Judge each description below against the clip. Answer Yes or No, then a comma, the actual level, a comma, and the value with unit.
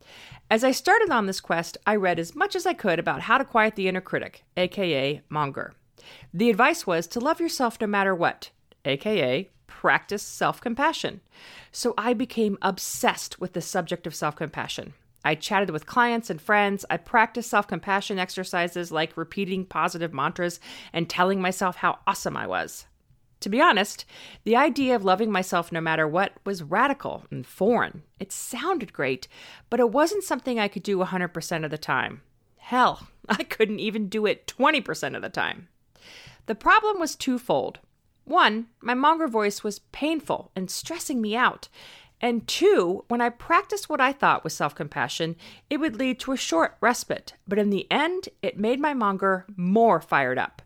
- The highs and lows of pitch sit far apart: Yes, wide, 6.1 semitones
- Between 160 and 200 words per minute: Yes, average, 175 wpm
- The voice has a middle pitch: No, high, 205 Hz